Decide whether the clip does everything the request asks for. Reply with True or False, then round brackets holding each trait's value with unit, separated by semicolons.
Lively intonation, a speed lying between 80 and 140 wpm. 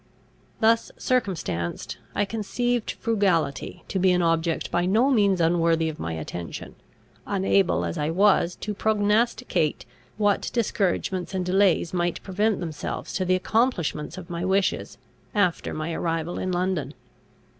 False (3.8 semitones; 135 wpm)